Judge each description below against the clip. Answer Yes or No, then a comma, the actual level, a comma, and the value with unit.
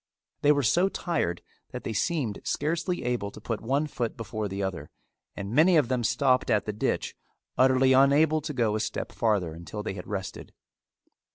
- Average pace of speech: Yes, average, 185 wpm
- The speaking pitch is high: No, low, 120 Hz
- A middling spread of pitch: No, wide, 5.9 semitones